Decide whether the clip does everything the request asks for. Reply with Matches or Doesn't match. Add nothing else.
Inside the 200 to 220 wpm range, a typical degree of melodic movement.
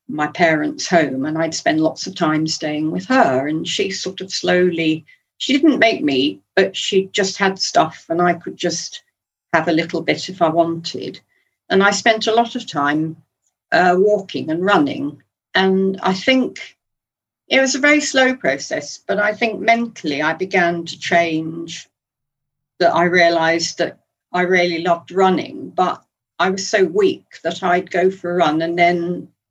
Doesn't match